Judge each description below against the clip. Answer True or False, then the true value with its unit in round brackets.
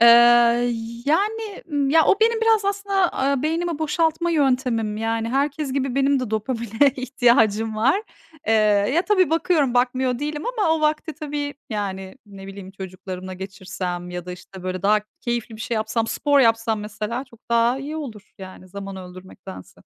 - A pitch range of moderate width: False (6.4 semitones)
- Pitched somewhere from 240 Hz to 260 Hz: True (245 Hz)